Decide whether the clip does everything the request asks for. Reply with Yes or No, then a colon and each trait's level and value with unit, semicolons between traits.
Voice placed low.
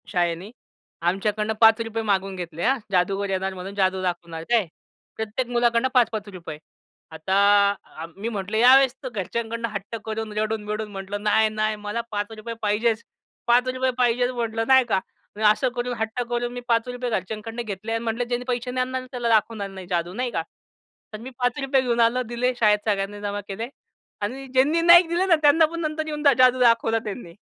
No: high, 225 Hz